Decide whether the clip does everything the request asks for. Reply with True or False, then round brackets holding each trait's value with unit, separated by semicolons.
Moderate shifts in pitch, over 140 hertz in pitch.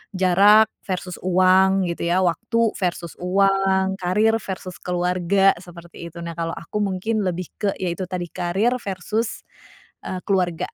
False (1.8 semitones; 185 Hz)